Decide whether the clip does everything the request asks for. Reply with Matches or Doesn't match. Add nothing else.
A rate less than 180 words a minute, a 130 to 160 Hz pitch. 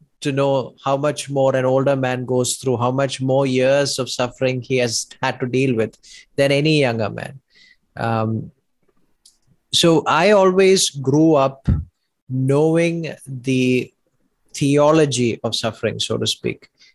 Matches